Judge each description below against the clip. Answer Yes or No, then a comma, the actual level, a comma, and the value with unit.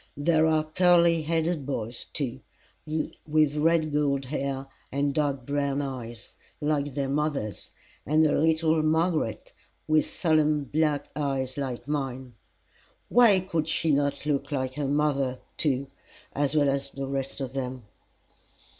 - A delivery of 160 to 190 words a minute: No, slow, 135 wpm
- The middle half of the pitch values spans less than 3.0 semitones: Yes, narrow, 2.4 semitones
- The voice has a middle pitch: Yes, medium, 145 Hz